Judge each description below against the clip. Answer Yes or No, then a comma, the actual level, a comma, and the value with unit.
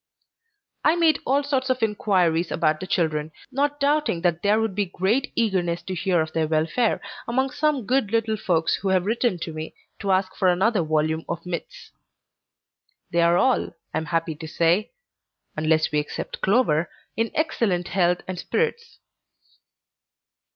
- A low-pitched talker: No, medium, 185 Hz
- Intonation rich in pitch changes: Yes, wide, 6.2 semitones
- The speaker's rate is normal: Yes, average, 165 wpm